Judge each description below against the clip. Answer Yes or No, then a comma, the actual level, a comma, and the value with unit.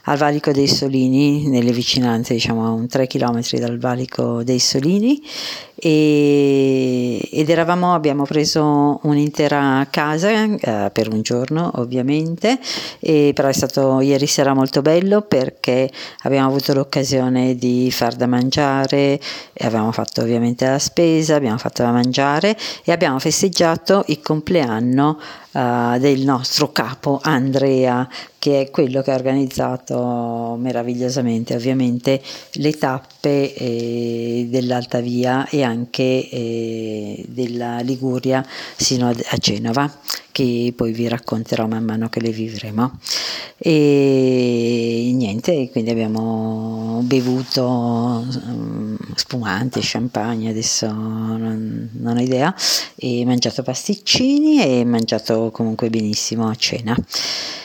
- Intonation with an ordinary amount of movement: Yes, average, 3.4 semitones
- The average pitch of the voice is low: Yes, low, 130 Hz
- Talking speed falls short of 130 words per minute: Yes, average, 120 wpm